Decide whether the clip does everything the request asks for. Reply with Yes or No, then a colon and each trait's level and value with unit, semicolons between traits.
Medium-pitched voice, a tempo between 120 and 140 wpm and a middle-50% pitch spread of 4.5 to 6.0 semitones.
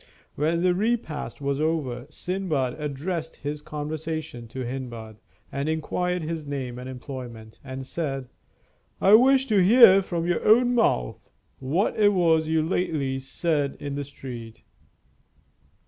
Yes: medium, 150 Hz; slow, 135 wpm; average, 5.1 semitones